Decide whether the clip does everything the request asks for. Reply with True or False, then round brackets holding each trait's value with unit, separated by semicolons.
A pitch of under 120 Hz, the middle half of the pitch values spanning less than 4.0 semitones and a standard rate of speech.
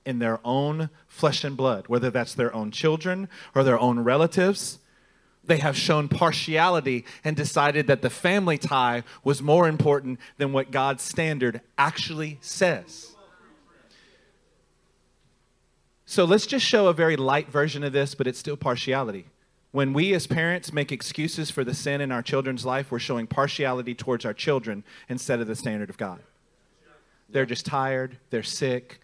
False (140 Hz; 3.6 semitones; 160 wpm)